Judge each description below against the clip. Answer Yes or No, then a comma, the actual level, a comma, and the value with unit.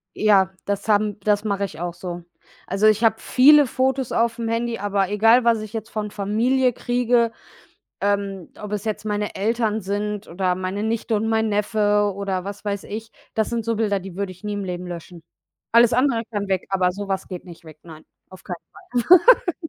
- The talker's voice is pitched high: Yes, high, 205 Hz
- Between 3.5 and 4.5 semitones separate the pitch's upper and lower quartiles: No, average, 2.7 semitones